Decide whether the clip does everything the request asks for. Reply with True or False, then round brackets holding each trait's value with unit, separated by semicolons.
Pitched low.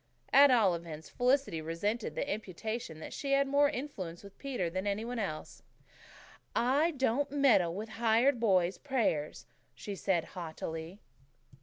False (215 Hz)